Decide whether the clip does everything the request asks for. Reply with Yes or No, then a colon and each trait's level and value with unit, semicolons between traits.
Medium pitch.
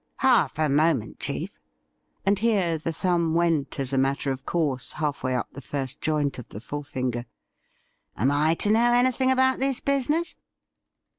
Yes: medium, 155 Hz